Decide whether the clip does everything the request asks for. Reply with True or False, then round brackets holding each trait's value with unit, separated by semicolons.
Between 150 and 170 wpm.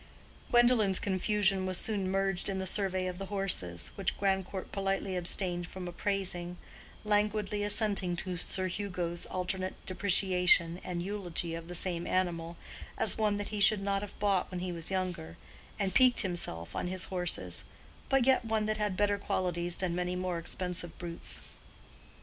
True (160 wpm)